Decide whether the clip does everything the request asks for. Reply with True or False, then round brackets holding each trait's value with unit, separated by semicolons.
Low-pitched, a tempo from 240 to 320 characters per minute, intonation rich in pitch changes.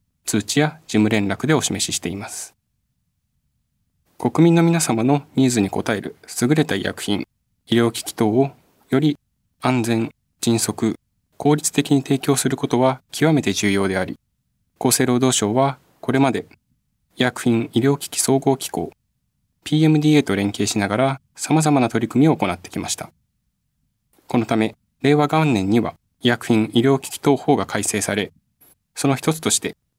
False (130 Hz; 290 characters per minute; 4.2 semitones)